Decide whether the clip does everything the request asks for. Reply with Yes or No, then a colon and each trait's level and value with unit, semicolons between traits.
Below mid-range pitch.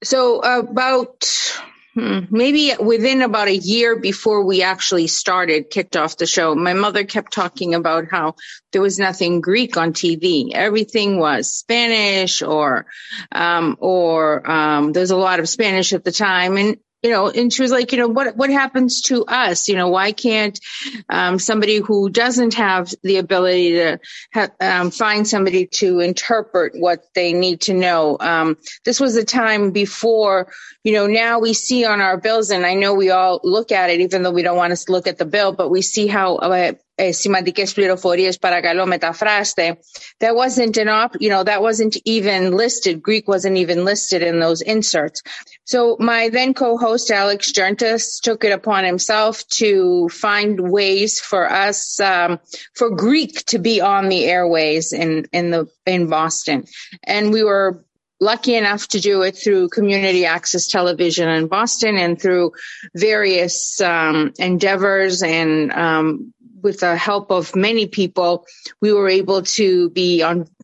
No: high, 195 Hz